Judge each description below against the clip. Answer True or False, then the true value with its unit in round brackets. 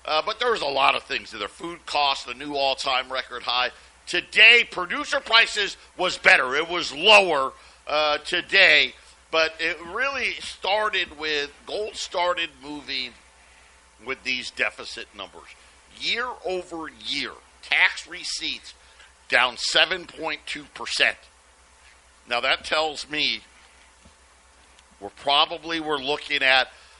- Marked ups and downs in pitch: True (8.9 semitones)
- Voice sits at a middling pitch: True (145 Hz)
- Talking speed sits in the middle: False (120 wpm)